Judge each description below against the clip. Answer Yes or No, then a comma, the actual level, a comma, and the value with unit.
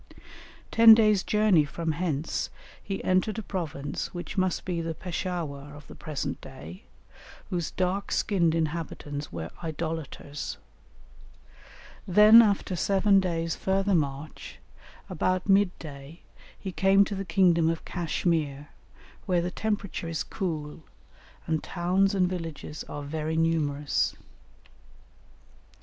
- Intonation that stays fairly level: No, average, 3.8 semitones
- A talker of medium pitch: Yes, medium, 170 Hz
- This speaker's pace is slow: Yes, slow, 120 wpm